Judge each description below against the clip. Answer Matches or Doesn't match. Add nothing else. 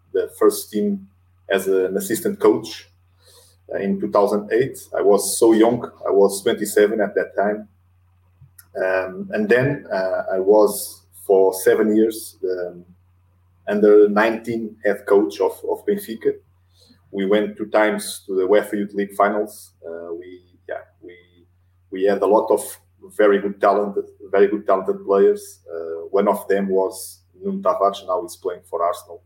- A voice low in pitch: Matches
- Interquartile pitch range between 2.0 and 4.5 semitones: Matches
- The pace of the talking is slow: Doesn't match